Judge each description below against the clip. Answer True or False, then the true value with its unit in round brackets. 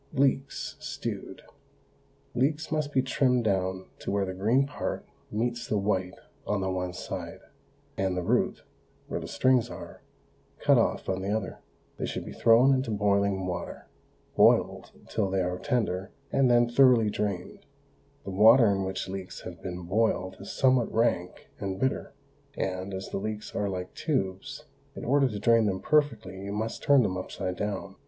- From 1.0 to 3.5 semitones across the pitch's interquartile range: False (4.4 semitones)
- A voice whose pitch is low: True (105 Hz)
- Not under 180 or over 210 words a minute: False (170 wpm)